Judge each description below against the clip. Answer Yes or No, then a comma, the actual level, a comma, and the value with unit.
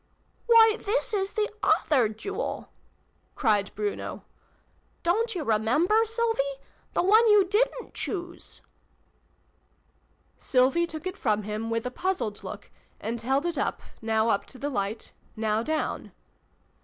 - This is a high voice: Yes, very high, 310 Hz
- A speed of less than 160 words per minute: Yes, average, 145 wpm